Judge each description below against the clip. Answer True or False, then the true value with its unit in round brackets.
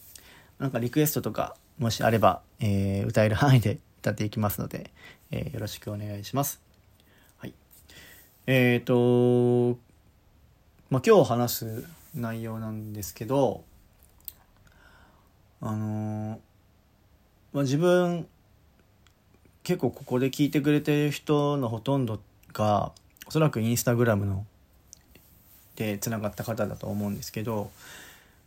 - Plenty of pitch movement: False (3.7 semitones)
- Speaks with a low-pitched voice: True (105 Hz)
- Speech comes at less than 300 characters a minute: True (250 characters per minute)